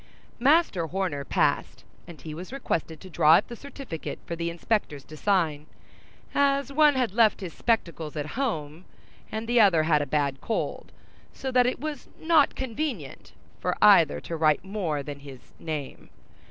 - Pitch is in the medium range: Yes, medium, 180 Hz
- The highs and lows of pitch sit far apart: Yes, wide, 8.4 semitones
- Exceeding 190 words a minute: No, average, 165 wpm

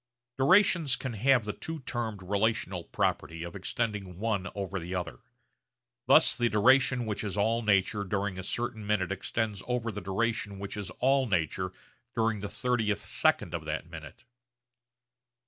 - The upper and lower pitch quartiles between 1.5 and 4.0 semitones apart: Yes, average, 3.6 semitones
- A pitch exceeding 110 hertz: No, low, 105 Hz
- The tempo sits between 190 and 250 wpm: No, average, 155 wpm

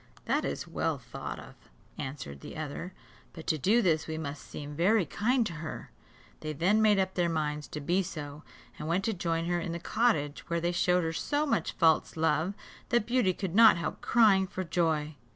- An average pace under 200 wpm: No, fast, 205 wpm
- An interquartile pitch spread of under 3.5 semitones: No, average, 3.8 semitones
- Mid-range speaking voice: Yes, medium, 170 Hz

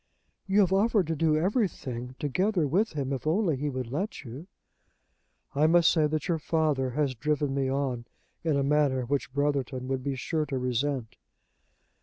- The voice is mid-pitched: Yes, medium, 145 Hz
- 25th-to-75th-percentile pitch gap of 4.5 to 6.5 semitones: No, average, 3.7 semitones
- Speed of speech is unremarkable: Yes, average, 175 wpm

